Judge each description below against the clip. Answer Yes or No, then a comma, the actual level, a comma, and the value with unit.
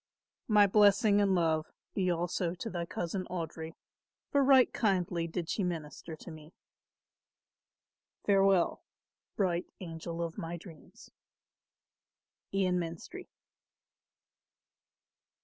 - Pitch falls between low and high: Yes, medium, 175 Hz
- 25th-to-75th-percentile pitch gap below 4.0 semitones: Yes, average, 3.0 semitones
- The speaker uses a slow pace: Yes, slow, 100 wpm